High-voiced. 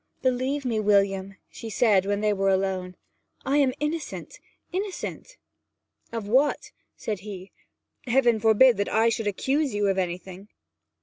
Yes: high, 215 Hz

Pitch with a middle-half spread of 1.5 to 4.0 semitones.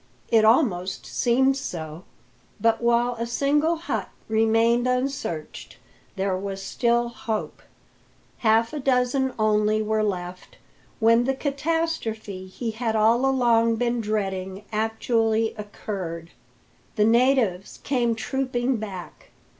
Yes: average, 2.9 semitones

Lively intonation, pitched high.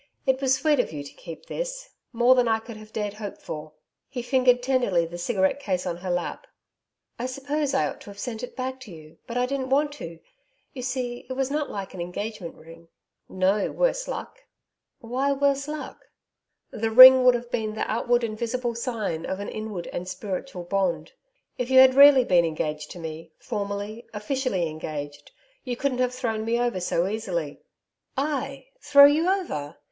Yes: wide, 6.0 semitones; high, 235 Hz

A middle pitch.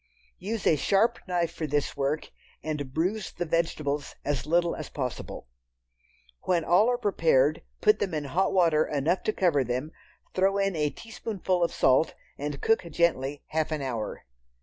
Yes: medium, 165 Hz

